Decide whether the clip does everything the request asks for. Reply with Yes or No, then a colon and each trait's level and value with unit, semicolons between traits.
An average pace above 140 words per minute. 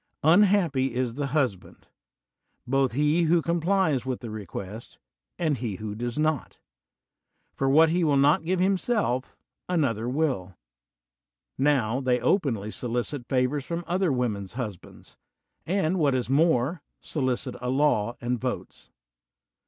No: slow, 135 wpm